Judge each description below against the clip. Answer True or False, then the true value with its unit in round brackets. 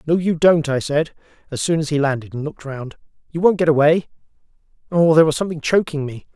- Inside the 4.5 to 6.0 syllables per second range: False (6.4 syllables/s)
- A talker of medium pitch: True (155 Hz)